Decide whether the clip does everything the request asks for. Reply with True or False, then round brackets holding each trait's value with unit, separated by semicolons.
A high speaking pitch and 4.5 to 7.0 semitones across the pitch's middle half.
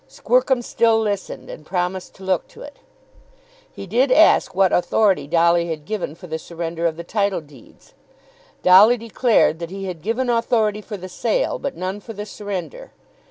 True (195 Hz; 4.8 semitones)